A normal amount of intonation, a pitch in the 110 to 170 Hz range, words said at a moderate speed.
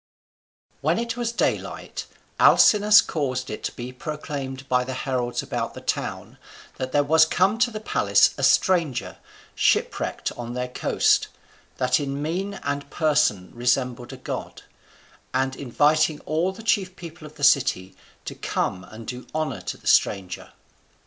Yes: average, 4.8 semitones; medium, 140 Hz; average, 155 wpm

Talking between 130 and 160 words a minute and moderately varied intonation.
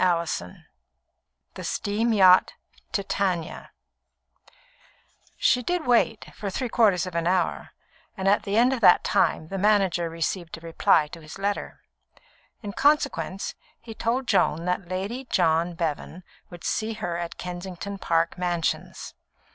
Yes: average, 140 wpm; average, 4.0 semitones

